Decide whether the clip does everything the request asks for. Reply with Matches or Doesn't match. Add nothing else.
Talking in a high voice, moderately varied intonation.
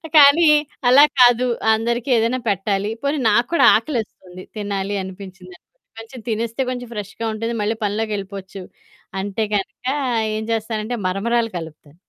Matches